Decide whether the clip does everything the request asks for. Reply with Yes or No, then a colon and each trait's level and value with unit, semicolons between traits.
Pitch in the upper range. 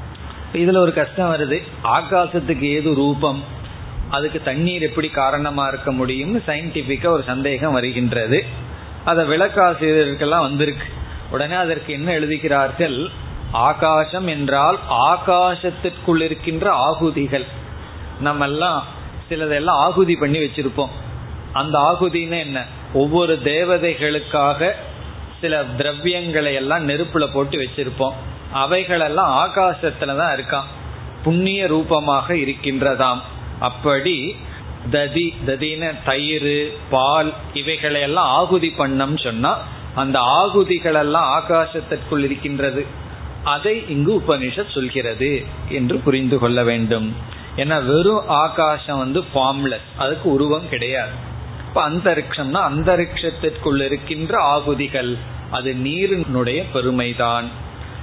No: medium, 145 Hz